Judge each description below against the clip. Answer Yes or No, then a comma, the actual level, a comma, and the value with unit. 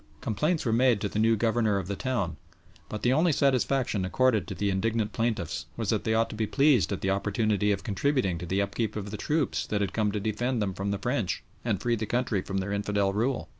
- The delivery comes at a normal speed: No, fast, 240 wpm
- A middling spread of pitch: Yes, average, 3.3 semitones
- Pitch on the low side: Yes, low, 110 Hz